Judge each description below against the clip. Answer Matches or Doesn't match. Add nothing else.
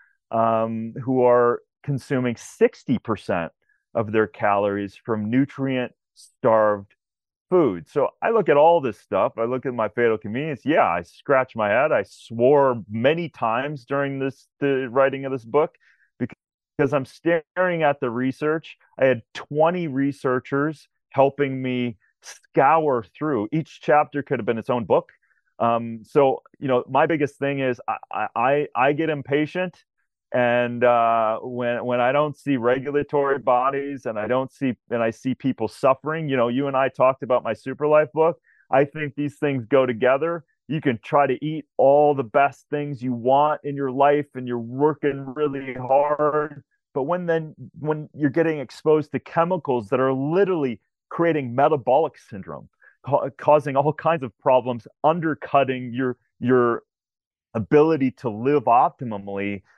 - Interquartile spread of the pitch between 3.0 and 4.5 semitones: Matches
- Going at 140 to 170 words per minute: Matches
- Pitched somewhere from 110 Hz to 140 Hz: Matches